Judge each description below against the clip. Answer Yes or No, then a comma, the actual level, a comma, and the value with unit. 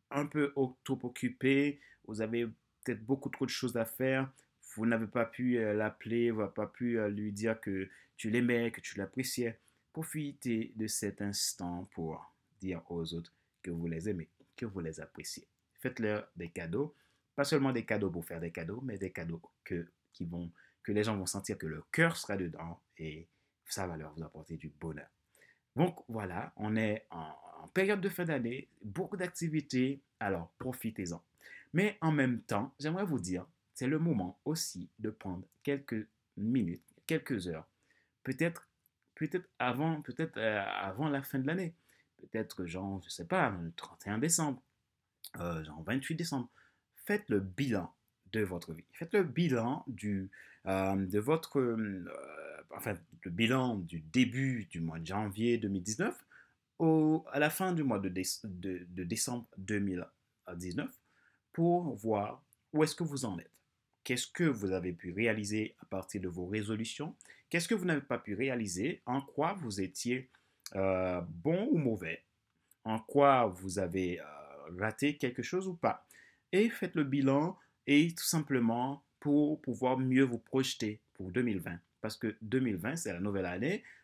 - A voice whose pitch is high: No, low, 115 Hz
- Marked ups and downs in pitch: Yes, wide, 6.5 semitones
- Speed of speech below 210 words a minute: Yes, average, 165 wpm